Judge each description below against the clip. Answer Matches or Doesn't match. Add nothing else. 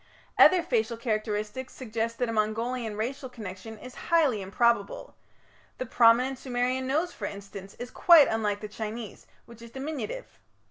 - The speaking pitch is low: Doesn't match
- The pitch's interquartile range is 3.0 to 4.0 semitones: Matches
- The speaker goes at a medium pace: Matches